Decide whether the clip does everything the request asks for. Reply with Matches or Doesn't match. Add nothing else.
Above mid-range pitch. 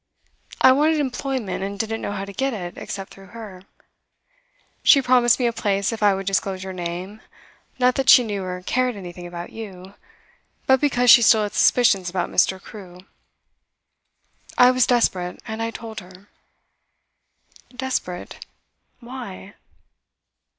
Matches